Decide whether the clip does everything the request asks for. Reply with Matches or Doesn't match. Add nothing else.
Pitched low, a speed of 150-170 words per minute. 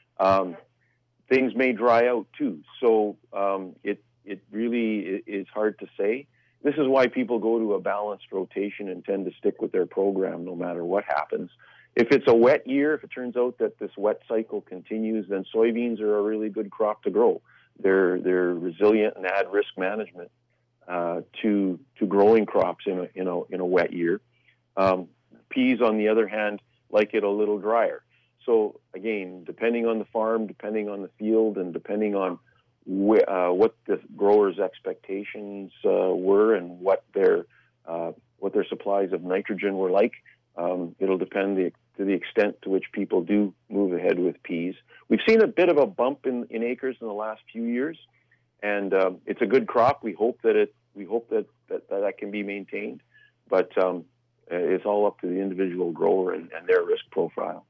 Doesn't match